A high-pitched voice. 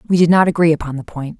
No: medium, 160 Hz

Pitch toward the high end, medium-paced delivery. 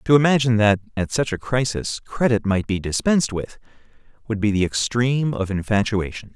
No: low, 115 Hz; average, 170 wpm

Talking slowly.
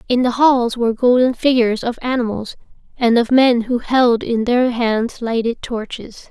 No: average, 170 wpm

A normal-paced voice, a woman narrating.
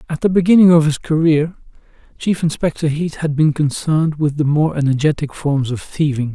No: average, 180 wpm; male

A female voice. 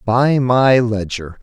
No: male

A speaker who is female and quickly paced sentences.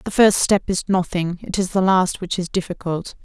Yes: female; fast, 220 wpm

